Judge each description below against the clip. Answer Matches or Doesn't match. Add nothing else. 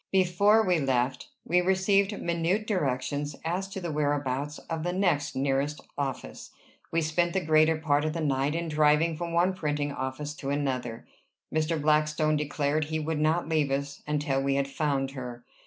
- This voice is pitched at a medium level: Matches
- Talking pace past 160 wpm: Matches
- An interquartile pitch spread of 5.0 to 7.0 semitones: Doesn't match